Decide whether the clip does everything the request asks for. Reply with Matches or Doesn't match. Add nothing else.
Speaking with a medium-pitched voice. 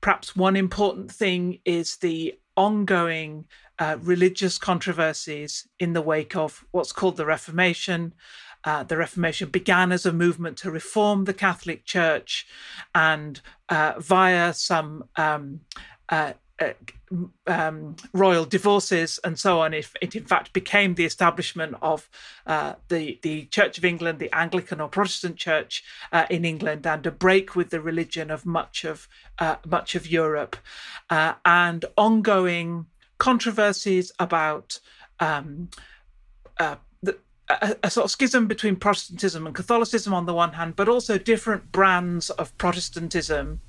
Matches